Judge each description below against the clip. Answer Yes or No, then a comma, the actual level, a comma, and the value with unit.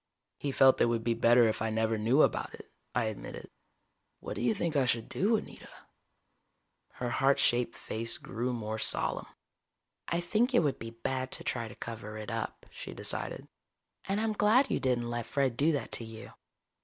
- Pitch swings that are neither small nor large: Yes, average, 4.1 semitones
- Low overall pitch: Yes, low, 120 Hz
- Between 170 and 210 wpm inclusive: Yes, average, 190 wpm